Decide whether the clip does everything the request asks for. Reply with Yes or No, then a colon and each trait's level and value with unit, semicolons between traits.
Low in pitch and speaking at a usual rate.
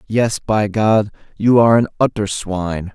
Yes: low, 105 Hz; average, 165 wpm